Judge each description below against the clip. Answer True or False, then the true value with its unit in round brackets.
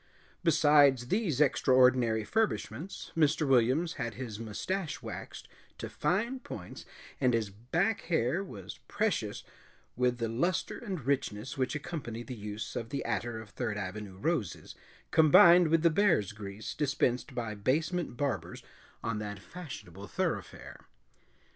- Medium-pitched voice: False (130 Hz)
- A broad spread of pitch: True (6.6 semitones)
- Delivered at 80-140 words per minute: True (135 wpm)